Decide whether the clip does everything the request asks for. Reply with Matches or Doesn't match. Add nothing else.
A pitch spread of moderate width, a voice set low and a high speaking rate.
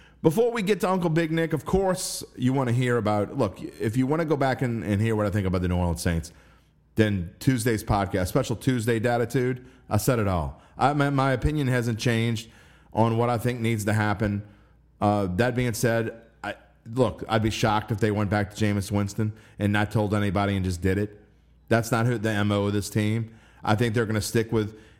Matches